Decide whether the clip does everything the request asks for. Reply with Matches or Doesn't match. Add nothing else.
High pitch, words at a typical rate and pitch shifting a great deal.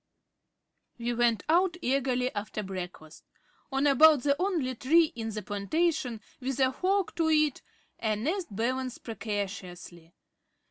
Doesn't match